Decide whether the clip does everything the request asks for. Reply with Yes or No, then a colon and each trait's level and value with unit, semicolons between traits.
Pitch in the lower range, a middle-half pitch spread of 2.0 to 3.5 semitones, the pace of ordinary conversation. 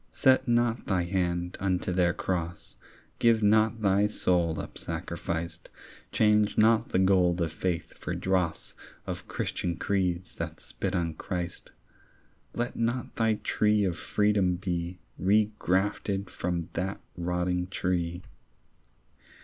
No: very low, 95 Hz; average, 3.1 semitones; slow, 125 wpm